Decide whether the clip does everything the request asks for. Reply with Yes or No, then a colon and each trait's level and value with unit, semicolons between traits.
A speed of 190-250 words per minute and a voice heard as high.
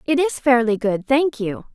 Yes: fast, 205 wpm; very high, 250 Hz